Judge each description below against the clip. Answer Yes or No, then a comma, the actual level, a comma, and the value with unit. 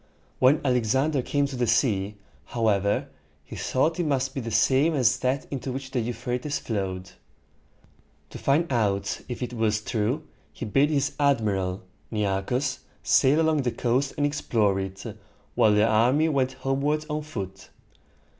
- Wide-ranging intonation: No, average, 4.6 semitones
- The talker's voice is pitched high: No, low, 125 Hz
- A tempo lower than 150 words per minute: No, average, 155 wpm